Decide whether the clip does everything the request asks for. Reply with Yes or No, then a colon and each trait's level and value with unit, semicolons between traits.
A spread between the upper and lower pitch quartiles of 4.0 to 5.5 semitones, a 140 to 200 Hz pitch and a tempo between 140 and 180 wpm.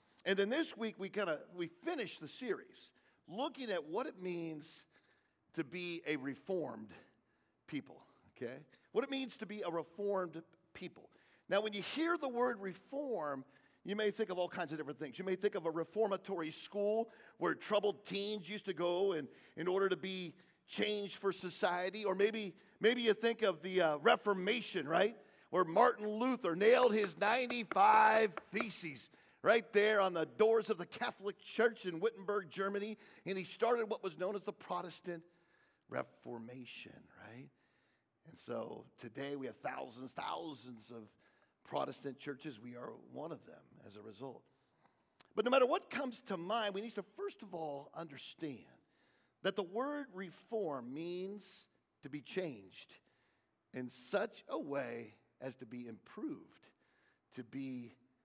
Yes: average, 4.8 semitones; high, 190 Hz; average, 160 wpm